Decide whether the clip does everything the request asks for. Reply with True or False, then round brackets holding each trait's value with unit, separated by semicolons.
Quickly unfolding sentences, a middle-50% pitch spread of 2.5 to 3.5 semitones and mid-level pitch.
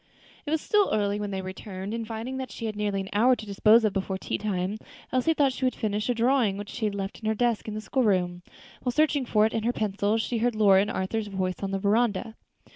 False (260 wpm; 3.2 semitones; 215 Hz)